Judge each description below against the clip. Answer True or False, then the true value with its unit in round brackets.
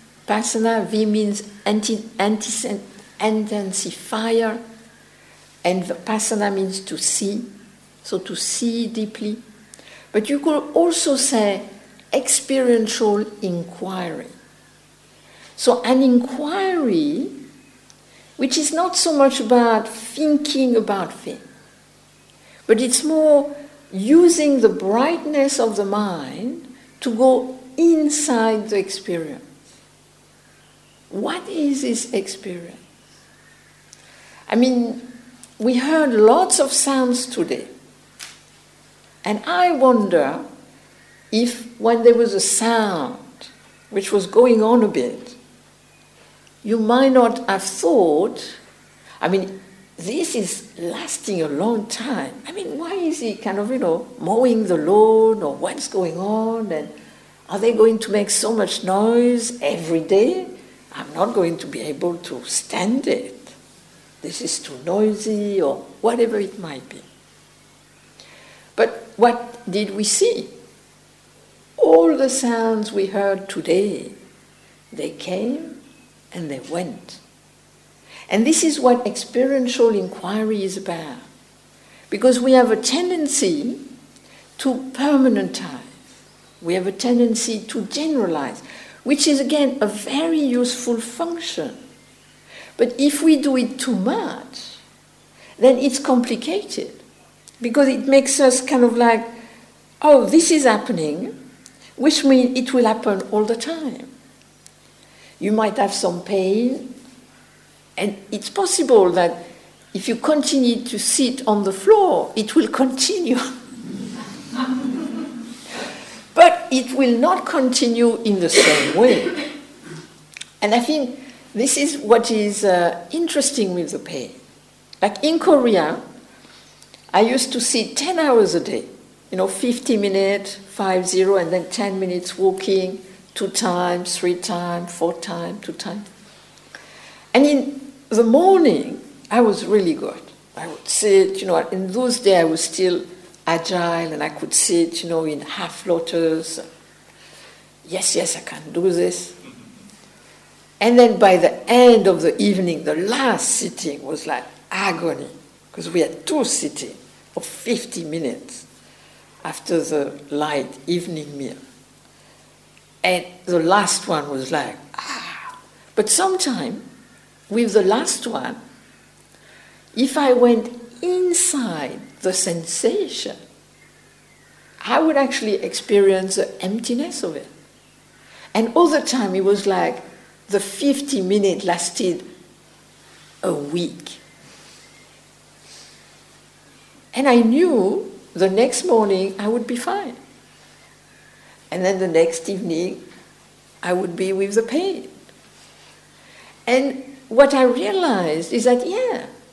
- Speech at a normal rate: False (120 wpm)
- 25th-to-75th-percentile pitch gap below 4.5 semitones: False (5.3 semitones)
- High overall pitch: True (230 Hz)